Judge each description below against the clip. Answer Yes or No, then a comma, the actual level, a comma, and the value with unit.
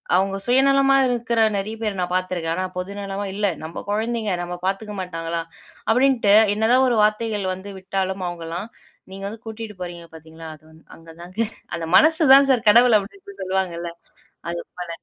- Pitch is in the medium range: No, high, 195 Hz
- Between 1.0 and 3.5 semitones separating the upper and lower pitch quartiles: No, average, 4.3 semitones